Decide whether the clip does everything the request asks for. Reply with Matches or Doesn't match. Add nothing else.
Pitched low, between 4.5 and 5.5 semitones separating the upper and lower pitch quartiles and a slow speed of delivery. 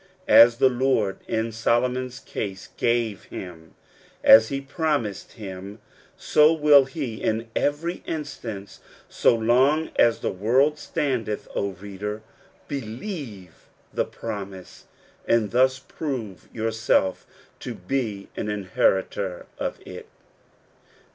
Matches